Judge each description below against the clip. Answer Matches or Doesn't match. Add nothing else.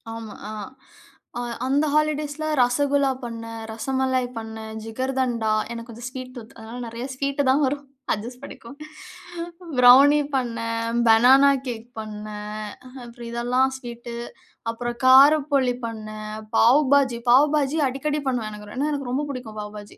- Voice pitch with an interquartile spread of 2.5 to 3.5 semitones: Matches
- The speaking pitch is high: Matches